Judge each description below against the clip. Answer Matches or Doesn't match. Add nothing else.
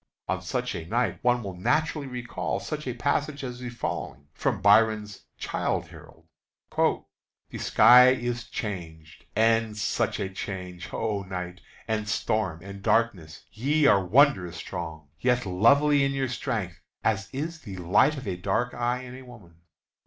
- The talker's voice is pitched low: Matches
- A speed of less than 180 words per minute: Matches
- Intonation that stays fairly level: Doesn't match